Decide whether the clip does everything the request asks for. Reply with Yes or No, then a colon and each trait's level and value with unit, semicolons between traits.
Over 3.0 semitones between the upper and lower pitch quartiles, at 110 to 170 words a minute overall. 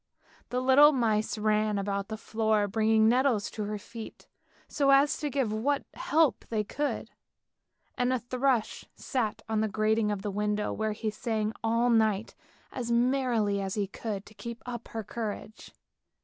No: average, 2.7 semitones; average, 165 wpm